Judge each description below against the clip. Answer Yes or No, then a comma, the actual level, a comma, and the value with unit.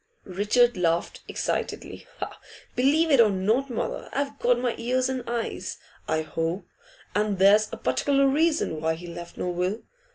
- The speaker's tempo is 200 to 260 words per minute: No, average, 155 wpm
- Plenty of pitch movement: Yes, wide, 6.4 semitones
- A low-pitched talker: No, high, 215 Hz